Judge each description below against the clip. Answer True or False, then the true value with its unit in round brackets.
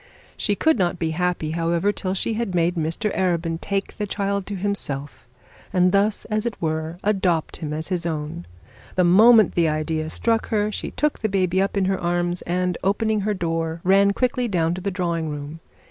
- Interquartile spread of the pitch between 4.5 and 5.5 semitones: False (3.5 semitones)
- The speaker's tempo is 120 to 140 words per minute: False (190 wpm)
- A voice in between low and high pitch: True (180 Hz)